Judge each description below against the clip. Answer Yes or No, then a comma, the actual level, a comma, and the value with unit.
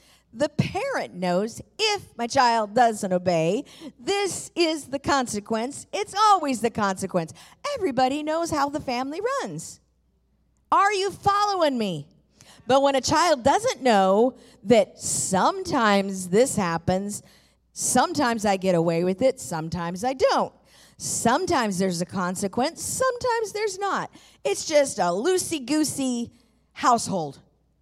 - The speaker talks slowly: Yes, slow, 125 wpm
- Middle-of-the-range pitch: No, very high, 255 Hz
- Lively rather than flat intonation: Yes, wide, 8.3 semitones